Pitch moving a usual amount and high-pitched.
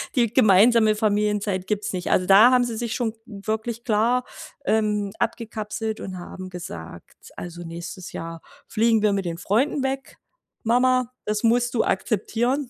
Yes: average, 3.6 semitones; high, 215 Hz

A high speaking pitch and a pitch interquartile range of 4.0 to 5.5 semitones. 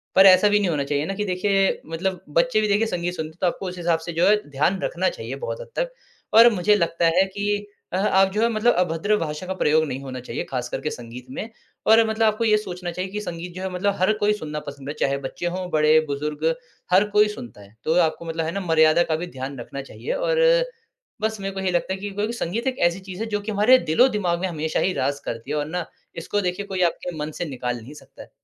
No: medium, 180 Hz; average, 4.8 semitones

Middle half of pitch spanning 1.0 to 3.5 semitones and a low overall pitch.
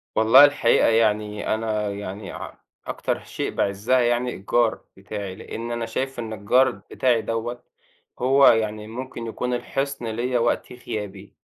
Yes: narrow, 2.6 semitones; low, 115 Hz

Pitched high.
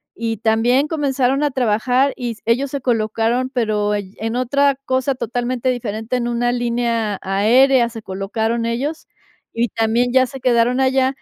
Yes: high, 240 Hz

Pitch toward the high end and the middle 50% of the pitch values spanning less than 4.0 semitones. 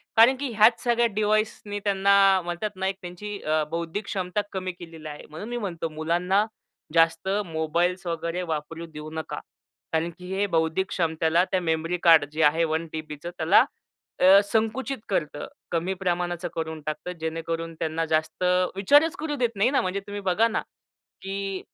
No: medium, 180 Hz; average, 3.6 semitones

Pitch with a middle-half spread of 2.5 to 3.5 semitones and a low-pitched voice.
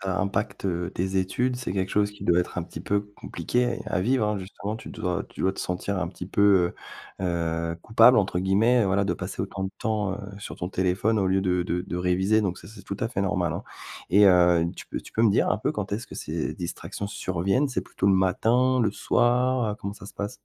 Yes: average, 2.8 semitones; very low, 95 Hz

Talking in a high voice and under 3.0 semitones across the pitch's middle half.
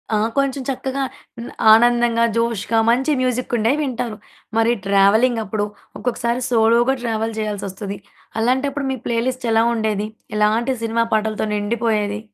Yes: high, 230 Hz; narrow, 2.4 semitones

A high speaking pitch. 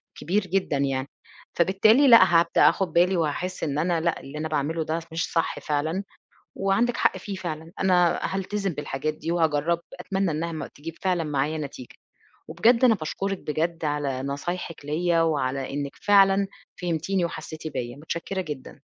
No: medium, 165 Hz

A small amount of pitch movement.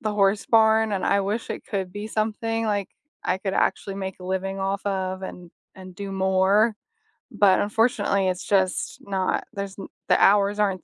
Yes: narrow, 1.8 semitones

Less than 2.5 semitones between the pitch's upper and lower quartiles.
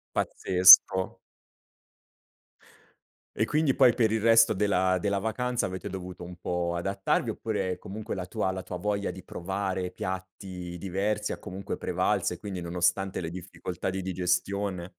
Yes: narrow, 2.1 semitones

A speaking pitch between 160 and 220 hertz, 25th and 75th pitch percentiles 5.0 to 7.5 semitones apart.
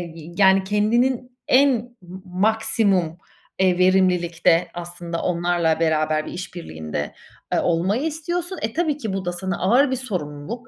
Yes: high, 190 Hz; wide, 5.5 semitones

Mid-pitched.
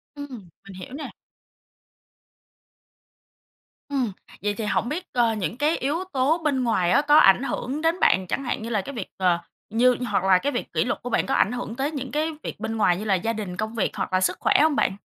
No: high, 235 Hz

